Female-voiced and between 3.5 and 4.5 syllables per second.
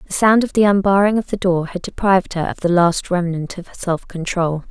No: female; 5.4 syllables/s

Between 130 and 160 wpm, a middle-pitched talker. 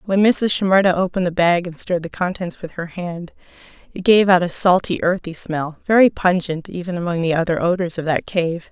No: fast, 205 wpm; medium, 175 Hz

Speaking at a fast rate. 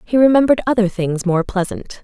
No: average, 175 wpm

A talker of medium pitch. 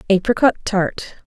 No: high, 195 Hz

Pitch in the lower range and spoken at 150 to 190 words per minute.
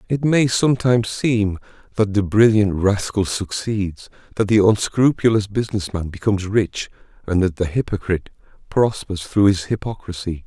No: low, 100 Hz; average, 140 wpm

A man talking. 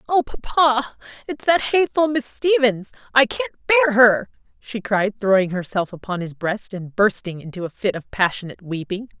No: female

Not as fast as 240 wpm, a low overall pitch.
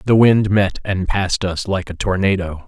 Yes: average, 200 wpm; very low, 95 Hz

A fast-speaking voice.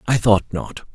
No: average, 190 wpm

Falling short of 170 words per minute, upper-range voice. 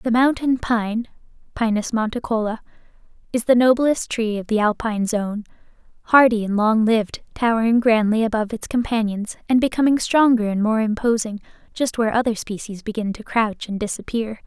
Yes: average, 150 wpm; high, 225 Hz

